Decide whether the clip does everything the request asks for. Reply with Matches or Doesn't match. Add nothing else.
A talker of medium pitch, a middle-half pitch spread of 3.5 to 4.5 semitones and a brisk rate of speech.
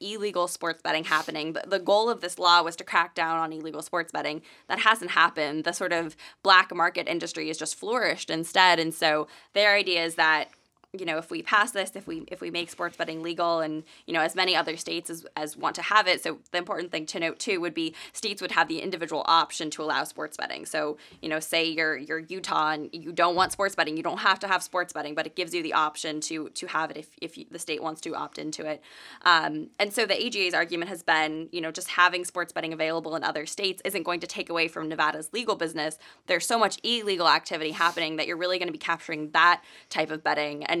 Doesn't match